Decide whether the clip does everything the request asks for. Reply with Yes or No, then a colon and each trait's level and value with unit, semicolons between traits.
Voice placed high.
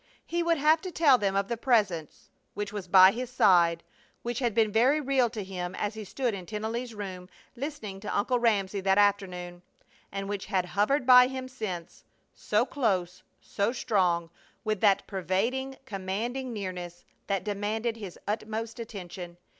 Yes: high, 210 Hz